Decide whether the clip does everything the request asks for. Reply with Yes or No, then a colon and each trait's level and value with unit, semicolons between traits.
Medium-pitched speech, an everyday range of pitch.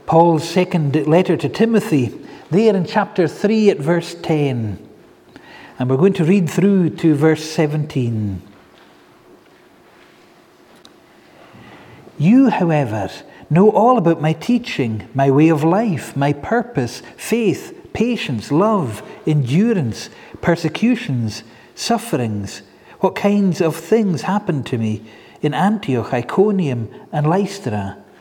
No: medium, 160 Hz; wide, 7.3 semitones